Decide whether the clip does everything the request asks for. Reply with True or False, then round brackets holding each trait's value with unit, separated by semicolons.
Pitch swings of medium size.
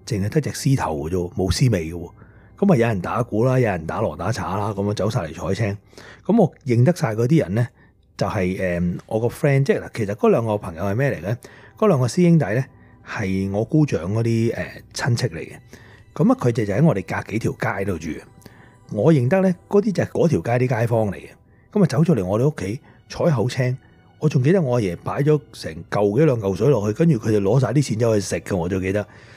False (5.8 semitones)